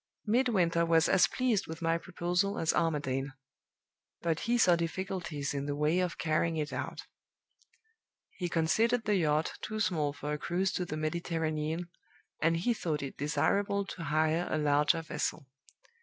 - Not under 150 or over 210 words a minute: Yes, average, 155 wpm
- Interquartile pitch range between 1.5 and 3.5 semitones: Yes, average, 3.2 semitones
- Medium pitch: Yes, medium, 165 Hz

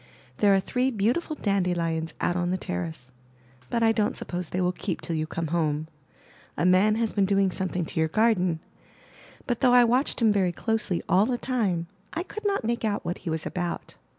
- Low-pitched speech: No, high, 190 Hz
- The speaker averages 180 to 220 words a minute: Yes, fast, 205 wpm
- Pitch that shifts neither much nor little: Yes, average, 4.8 semitones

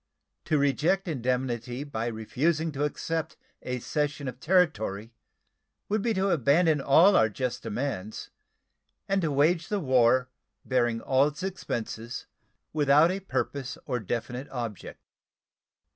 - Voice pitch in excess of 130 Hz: Yes, medium, 140 Hz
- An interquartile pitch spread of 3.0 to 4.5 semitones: No, average, 5.1 semitones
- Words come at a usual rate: No, slow, 130 wpm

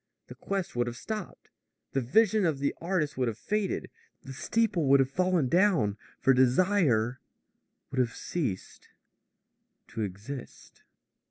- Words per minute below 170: Yes, average, 140 wpm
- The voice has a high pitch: No, medium, 140 Hz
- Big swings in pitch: Yes, wide, 7.1 semitones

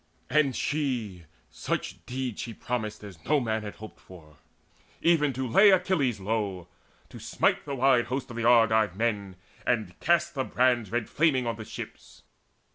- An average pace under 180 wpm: Yes, average, 165 wpm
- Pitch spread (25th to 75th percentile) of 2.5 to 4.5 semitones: Yes, average, 4.1 semitones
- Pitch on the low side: Yes, low, 120 Hz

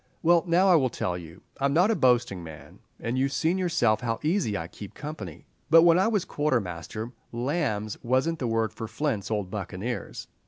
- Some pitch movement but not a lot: No, wide, 7.4 semitones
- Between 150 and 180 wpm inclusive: No, average, 190 wpm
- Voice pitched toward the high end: No, low, 120 Hz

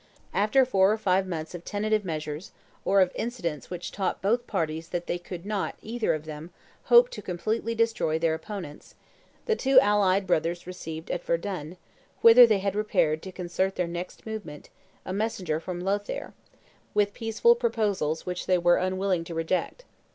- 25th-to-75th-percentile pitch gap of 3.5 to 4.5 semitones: Yes, average, 4.1 semitones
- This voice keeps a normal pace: Yes, average, 170 wpm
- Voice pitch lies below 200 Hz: Yes, medium, 185 Hz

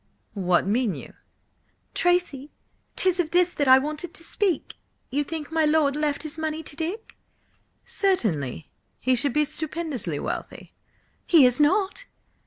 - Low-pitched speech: No, very high, 300 Hz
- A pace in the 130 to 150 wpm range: Yes, average, 145 wpm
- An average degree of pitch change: Yes, average, 4.3 semitones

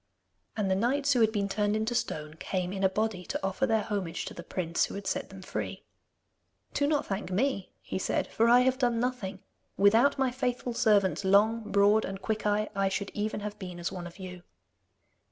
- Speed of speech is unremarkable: No, fast, 210 wpm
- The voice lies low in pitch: No, high, 205 Hz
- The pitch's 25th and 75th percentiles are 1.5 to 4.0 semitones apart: Yes, average, 3.5 semitones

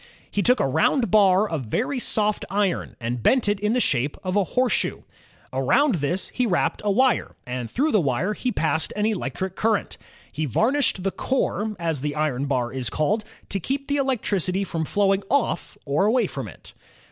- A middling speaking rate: Yes, average, 195 wpm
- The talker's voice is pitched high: Yes, high, 195 Hz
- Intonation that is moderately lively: No, wide, 7.2 semitones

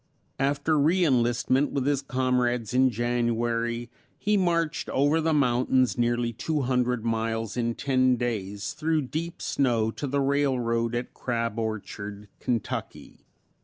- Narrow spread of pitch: No, average, 3.2 semitones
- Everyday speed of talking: No, slow, 130 wpm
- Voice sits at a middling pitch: No, low, 125 Hz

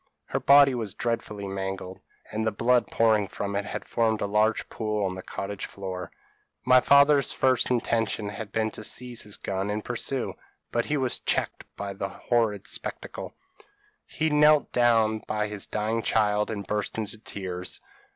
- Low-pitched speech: Yes, low, 110 Hz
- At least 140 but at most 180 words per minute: Yes, average, 170 wpm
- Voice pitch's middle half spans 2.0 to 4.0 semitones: Yes, average, 2.9 semitones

